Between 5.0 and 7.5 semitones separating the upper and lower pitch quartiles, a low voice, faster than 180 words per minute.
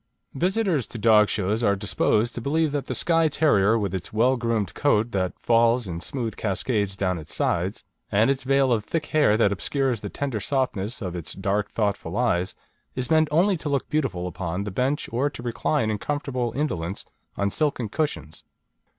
Yes: wide, 5.6 semitones; low, 115 Hz; average, 190 wpm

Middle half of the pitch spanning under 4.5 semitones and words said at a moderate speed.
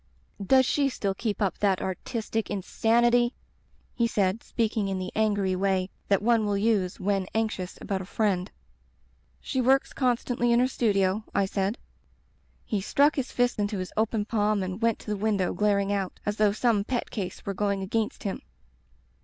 Yes: average, 2.9 semitones; average, 180 wpm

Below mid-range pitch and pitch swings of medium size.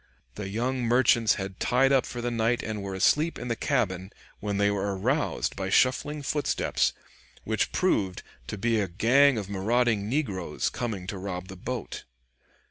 Yes: low, 110 Hz; average, 4.3 semitones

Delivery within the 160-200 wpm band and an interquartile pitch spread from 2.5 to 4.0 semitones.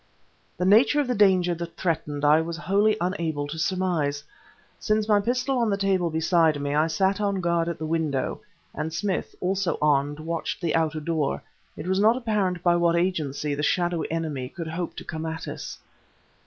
Yes: average, 190 wpm; average, 3.5 semitones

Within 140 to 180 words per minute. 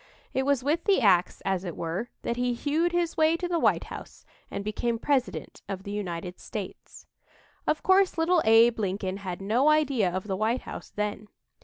No: average, 190 wpm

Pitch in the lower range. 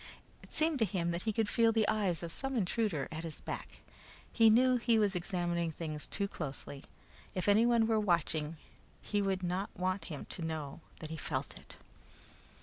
No: medium, 185 Hz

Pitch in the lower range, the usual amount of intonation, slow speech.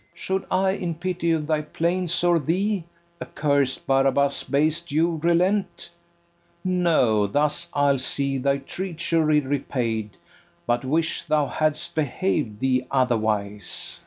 No: medium, 150 Hz; average, 4.3 semitones; slow, 125 wpm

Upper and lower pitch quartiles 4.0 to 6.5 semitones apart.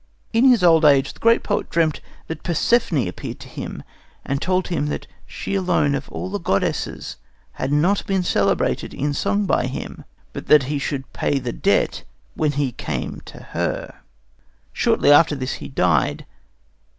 Yes: average, 5.0 semitones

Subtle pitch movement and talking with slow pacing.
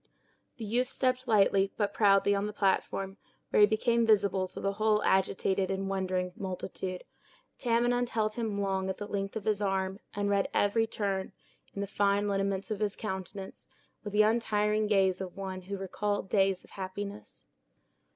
No: narrow, 1.7 semitones; average, 170 wpm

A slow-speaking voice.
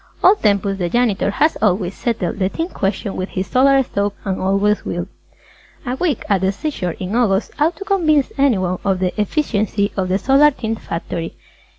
No: average, 185 wpm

